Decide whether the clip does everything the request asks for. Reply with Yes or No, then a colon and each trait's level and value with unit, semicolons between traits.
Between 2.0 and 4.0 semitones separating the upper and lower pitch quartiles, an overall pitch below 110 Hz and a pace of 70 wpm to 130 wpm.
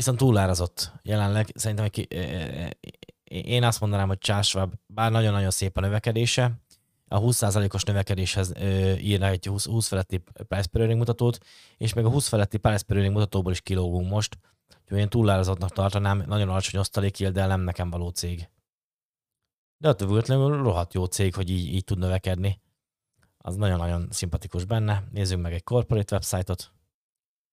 No: average, 2.9 semitones; low, 100 Hz; fast, 155 wpm